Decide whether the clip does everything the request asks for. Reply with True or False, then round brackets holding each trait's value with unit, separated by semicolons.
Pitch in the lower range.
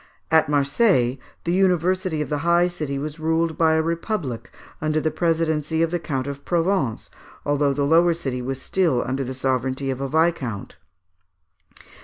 False (155 Hz)